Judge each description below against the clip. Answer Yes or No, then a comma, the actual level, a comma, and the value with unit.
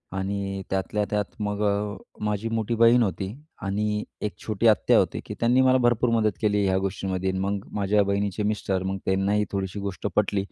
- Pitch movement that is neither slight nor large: No, narrow, 1.5 semitones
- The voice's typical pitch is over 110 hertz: No, low, 100 Hz